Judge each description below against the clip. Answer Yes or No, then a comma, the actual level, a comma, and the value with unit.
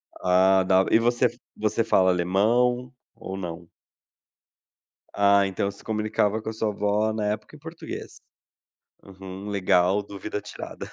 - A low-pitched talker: Yes, low, 100 Hz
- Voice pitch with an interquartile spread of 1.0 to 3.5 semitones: Yes, narrow, 2.6 semitones